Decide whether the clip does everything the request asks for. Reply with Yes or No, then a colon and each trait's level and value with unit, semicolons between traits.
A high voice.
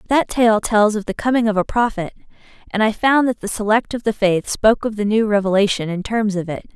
Yes: high, 215 Hz